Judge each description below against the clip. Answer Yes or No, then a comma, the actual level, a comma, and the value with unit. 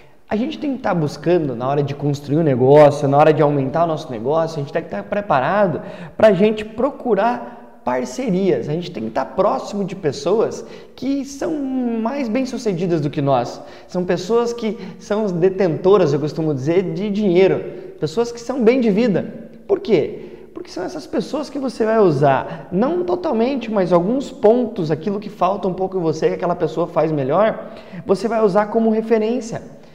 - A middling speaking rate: No, fast, 190 wpm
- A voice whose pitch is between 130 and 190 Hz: No, high, 205 Hz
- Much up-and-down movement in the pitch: Yes, wide, 6.1 semitones